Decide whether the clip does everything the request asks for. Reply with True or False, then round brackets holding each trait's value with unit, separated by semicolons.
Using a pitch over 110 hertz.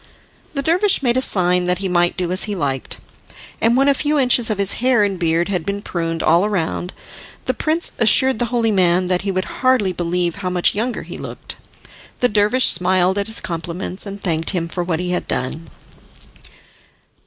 True (190 Hz)